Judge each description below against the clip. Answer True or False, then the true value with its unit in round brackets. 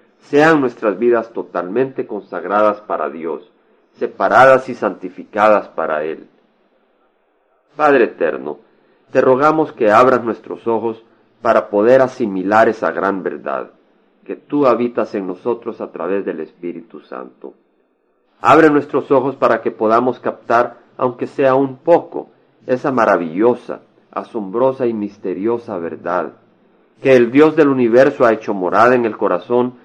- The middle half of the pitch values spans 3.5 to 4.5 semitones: True (3.8 semitones)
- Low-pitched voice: True (120 Hz)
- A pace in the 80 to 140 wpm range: True (130 wpm)